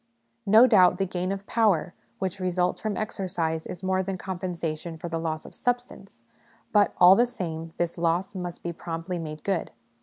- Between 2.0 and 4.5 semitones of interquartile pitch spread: Yes, average, 2.9 semitones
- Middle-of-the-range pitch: Yes, medium, 180 Hz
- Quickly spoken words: No, average, 185 wpm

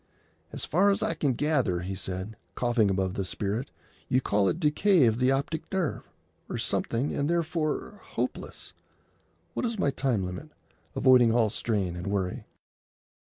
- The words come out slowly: No, average, 160 wpm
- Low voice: Yes, low, 125 Hz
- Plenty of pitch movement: Yes, wide, 7.4 semitones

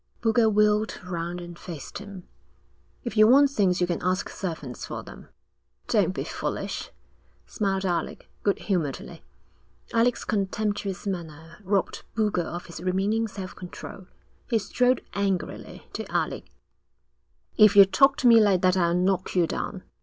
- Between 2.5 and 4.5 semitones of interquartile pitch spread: Yes, average, 3.2 semitones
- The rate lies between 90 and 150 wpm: Yes, average, 145 wpm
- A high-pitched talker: Yes, high, 195 Hz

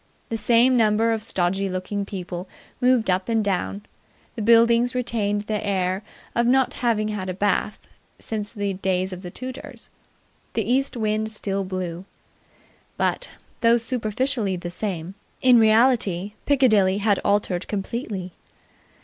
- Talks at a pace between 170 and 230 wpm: No, average, 140 wpm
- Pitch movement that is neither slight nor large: Yes, average, 3.5 semitones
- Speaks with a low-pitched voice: No, high, 210 Hz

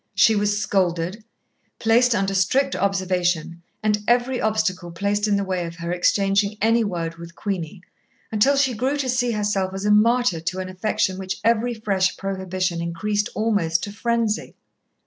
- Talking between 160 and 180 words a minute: Yes, average, 165 wpm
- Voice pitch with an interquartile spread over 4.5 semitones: No, average, 3.1 semitones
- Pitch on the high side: Yes, high, 200 Hz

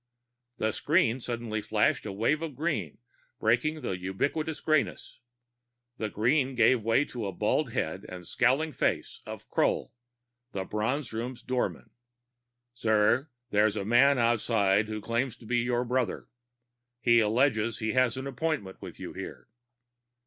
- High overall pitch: No, low, 120 Hz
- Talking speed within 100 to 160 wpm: Yes, average, 150 wpm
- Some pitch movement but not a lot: Yes, average, 3.6 semitones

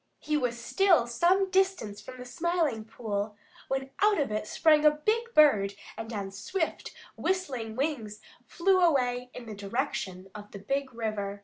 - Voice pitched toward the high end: Yes, very high, 250 Hz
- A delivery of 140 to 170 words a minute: Yes, average, 165 wpm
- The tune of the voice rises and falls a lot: Yes, wide, 7.2 semitones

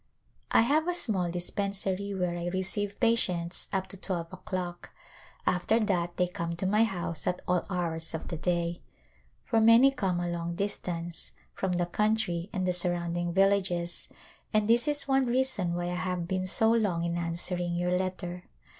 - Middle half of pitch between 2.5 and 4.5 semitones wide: Yes, average, 2.8 semitones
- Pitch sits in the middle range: Yes, medium, 180 Hz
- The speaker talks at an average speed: Yes, average, 175 wpm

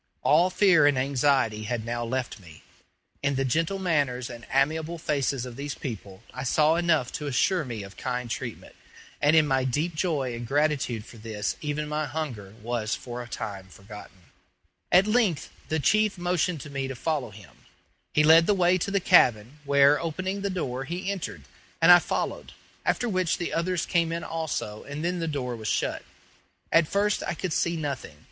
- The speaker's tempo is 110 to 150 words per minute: No, average, 190 wpm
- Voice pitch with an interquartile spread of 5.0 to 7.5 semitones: Yes, wide, 5.6 semitones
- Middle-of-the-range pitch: Yes, medium, 145 Hz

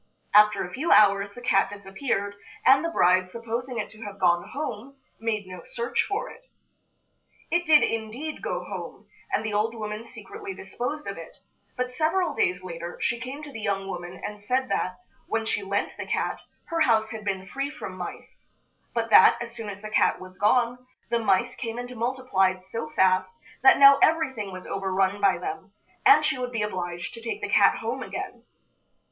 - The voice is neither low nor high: No, high, 220 Hz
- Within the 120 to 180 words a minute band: No, average, 190 wpm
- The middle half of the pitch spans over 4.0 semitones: Yes, average, 4.7 semitones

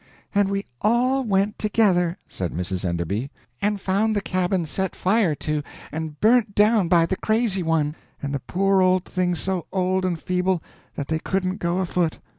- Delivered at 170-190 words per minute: Yes, average, 175 wpm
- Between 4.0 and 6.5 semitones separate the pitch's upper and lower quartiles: No, average, 3.6 semitones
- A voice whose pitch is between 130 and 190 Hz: Yes, medium, 185 Hz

